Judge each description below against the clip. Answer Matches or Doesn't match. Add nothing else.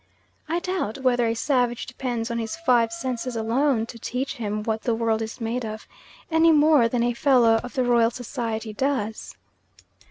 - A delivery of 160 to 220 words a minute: Matches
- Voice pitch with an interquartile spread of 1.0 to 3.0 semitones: Matches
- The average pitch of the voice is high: Matches